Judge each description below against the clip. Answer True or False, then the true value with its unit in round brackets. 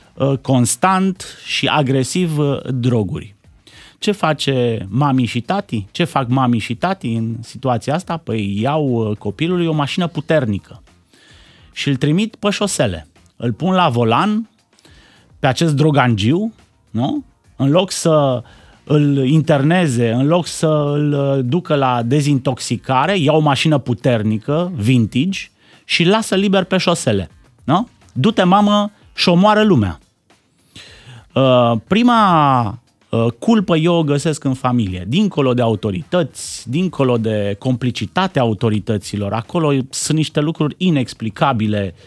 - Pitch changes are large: True (6.4 semitones)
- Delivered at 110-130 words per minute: True (120 wpm)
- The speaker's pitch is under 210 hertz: True (135 Hz)